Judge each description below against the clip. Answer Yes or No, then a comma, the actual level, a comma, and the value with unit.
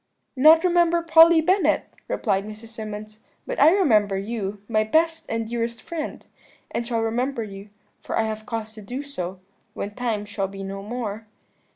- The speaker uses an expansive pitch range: Yes, wide, 5.8 semitones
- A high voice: Yes, high, 225 Hz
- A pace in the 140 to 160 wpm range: No, average, 170 wpm